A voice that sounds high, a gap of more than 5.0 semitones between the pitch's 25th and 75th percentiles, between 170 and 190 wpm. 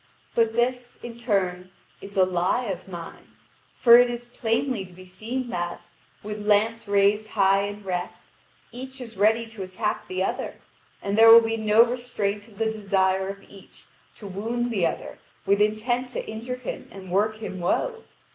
No: high, 210 Hz; average, 3.3 semitones; average, 175 wpm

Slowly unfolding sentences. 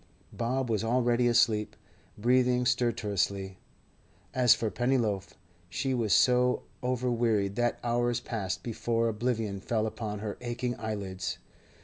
Yes: slow, 115 wpm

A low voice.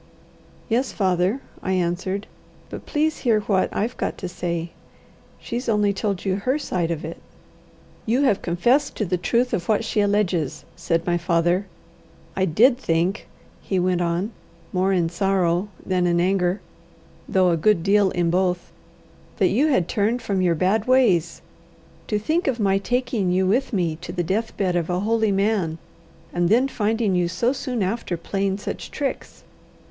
No: high, 195 Hz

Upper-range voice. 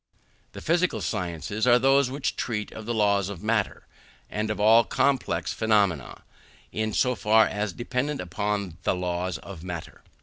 No: low, 105 Hz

